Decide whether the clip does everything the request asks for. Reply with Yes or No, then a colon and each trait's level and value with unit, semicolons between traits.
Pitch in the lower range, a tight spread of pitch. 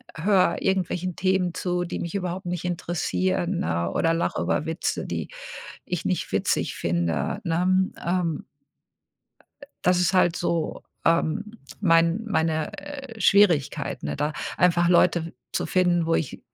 No: medium, 175 Hz; narrow, 2.1 semitones